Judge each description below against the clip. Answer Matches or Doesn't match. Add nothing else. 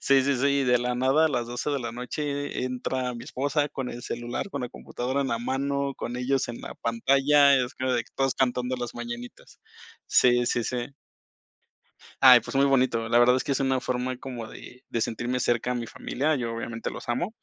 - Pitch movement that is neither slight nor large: Doesn't match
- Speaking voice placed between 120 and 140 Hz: Matches